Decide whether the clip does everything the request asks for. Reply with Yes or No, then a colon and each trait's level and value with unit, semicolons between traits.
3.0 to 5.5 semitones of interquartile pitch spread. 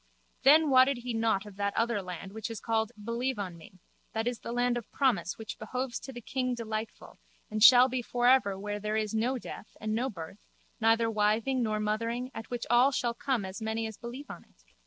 No: narrow, 2.6 semitones